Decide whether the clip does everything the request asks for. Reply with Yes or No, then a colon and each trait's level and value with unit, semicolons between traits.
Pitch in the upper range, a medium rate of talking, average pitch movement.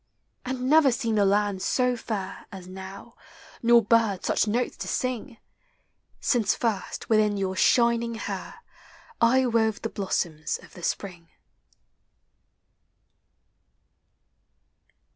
No: high, 220 Hz; slow, 110 wpm; average, 3.4 semitones